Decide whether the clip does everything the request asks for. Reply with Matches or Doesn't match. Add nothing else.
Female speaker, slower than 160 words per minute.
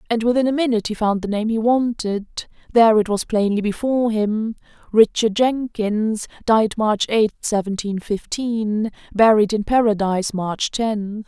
Matches